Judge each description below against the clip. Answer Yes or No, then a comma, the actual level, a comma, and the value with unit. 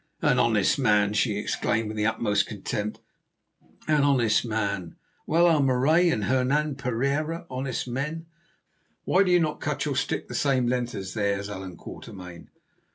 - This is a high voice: No, low, 125 Hz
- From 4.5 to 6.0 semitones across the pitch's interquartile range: Yes, wide, 5.6 semitones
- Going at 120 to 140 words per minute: No, average, 160 wpm